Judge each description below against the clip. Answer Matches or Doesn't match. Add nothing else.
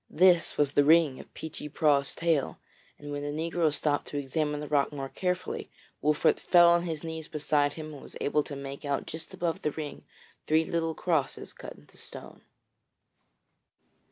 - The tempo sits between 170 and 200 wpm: Matches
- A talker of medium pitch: Matches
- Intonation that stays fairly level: Matches